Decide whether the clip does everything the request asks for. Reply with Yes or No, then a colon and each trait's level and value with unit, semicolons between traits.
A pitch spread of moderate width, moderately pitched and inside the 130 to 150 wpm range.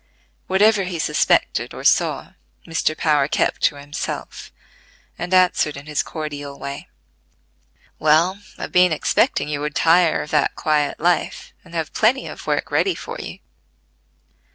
Yes: average, 3.4 semitones; medium, 160 Hz; average, 145 wpm